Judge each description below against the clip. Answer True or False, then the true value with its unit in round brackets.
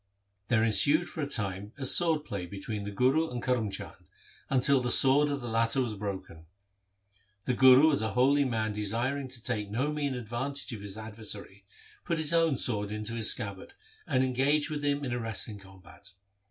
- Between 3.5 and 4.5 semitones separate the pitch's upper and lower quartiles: False (4.9 semitones)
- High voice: False (120 Hz)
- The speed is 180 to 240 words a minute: True (190 wpm)